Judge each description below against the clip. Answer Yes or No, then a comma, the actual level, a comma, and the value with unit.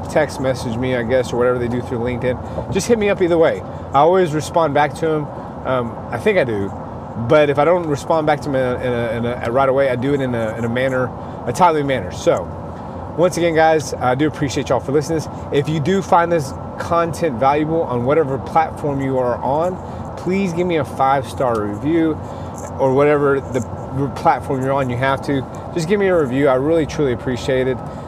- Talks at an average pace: No, fast, 225 wpm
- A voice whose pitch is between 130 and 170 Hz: Yes, low, 135 Hz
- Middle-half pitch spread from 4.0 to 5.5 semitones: Yes, average, 4.5 semitones